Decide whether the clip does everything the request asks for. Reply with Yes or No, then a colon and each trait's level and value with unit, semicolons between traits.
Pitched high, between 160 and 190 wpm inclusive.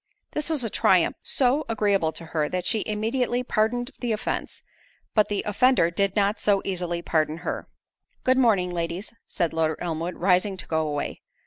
Yes: high, 200 Hz; average, 175 wpm